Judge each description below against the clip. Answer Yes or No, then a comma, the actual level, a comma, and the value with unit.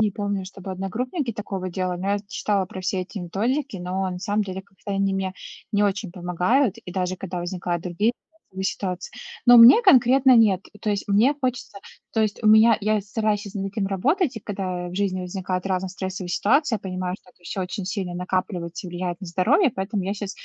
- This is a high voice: Yes, high, 195 Hz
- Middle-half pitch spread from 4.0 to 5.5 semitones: No, average, 2.7 semitones